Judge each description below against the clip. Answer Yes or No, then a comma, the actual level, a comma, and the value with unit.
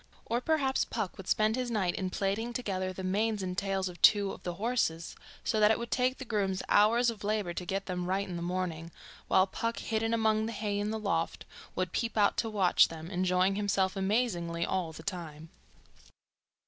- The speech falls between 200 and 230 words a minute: Yes, fast, 205 wpm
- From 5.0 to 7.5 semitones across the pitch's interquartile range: No, average, 3.2 semitones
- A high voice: Yes, high, 195 Hz